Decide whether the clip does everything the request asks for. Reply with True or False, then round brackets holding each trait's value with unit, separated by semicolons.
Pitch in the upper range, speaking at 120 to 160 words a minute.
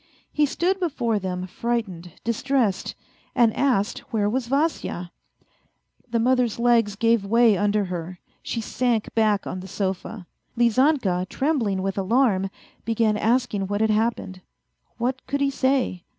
True (225 Hz; 135 wpm)